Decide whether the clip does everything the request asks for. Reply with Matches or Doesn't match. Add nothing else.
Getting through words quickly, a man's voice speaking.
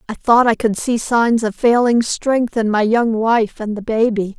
Doesn't match